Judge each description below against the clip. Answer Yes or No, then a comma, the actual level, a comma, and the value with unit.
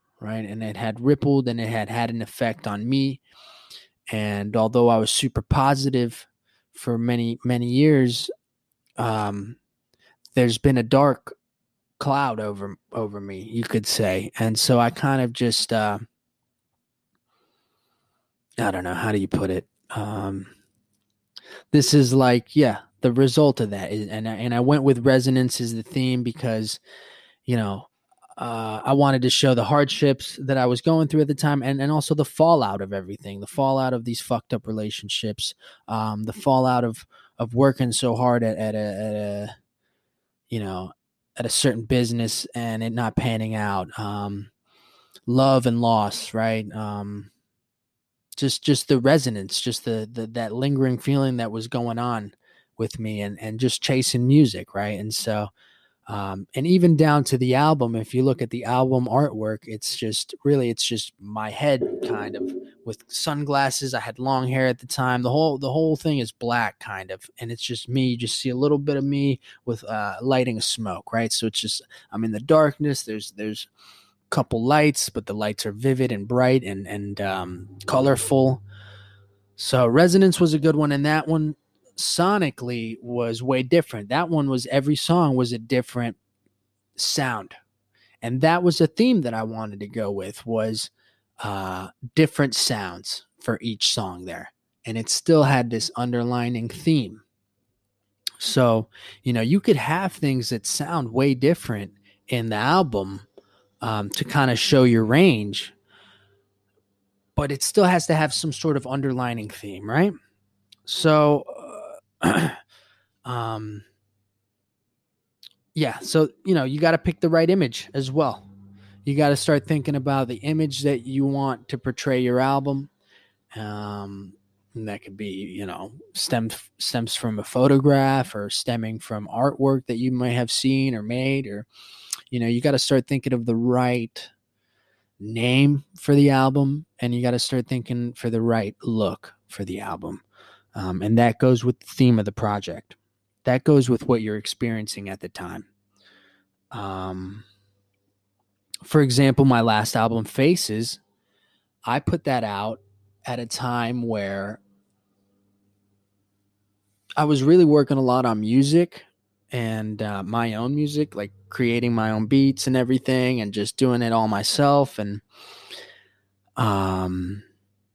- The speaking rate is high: No, average, 165 wpm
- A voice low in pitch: Yes, low, 120 Hz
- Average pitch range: Yes, average, 4.5 semitones